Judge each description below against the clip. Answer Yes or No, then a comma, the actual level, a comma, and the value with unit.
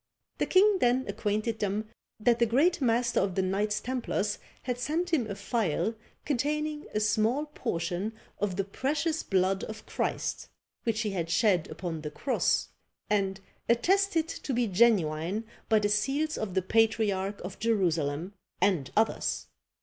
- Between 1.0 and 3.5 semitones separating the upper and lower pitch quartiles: No, average, 4.6 semitones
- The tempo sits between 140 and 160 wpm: Yes, average, 150 wpm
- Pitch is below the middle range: No, high, 215 Hz